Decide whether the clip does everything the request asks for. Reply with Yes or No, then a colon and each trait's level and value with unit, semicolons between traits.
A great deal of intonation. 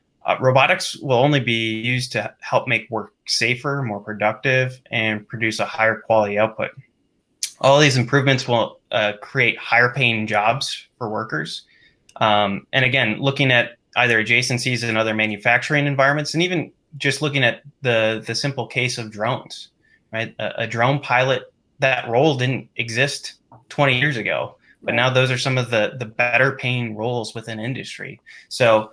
No: average, 3.4 semitones